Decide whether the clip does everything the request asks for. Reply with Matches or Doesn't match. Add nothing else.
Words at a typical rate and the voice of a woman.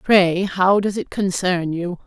Matches